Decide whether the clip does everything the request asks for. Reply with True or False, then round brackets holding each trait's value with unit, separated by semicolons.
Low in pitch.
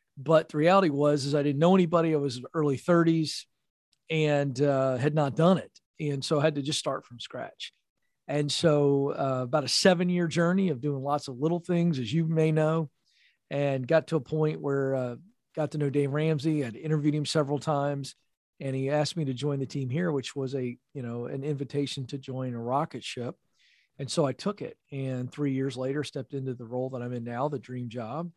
False (145 Hz)